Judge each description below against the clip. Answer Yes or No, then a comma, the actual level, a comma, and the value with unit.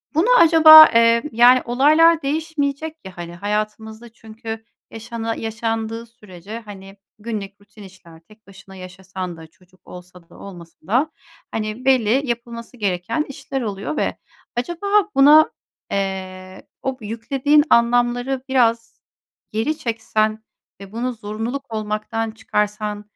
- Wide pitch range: No, average, 4.1 semitones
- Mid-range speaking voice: No, high, 225 Hz